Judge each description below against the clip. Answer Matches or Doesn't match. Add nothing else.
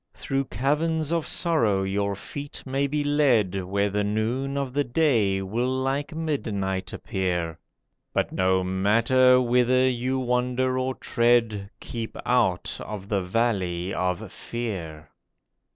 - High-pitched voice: Doesn't match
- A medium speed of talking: Doesn't match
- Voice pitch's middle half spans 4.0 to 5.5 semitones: Matches